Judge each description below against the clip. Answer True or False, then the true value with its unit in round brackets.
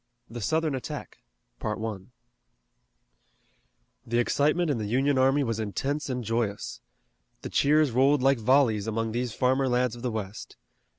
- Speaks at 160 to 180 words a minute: False (135 wpm)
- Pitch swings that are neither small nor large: True (3.6 semitones)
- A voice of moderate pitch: False (125 Hz)